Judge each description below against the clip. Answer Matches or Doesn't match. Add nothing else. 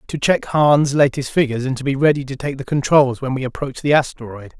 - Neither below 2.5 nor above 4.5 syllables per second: Doesn't match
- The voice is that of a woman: Doesn't match